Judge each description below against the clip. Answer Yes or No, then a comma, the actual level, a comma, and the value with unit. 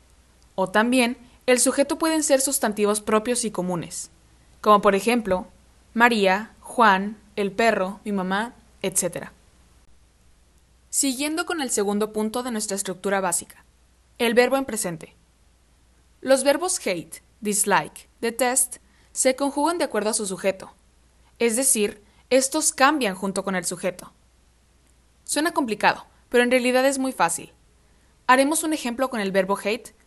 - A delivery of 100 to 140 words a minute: Yes, slow, 135 wpm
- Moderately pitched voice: No, high, 210 Hz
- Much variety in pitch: Yes, wide, 6.1 semitones